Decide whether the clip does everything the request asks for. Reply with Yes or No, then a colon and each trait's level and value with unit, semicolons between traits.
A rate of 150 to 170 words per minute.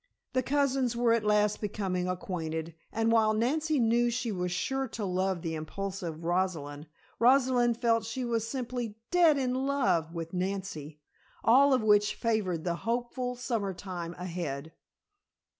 No: average, 140 wpm